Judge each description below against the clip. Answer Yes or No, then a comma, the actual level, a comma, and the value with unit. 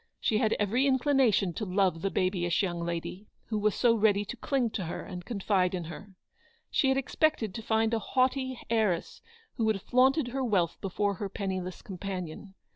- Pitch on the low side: No, high, 205 Hz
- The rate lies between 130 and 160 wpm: No, average, 190 wpm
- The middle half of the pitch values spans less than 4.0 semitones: No, average, 4.4 semitones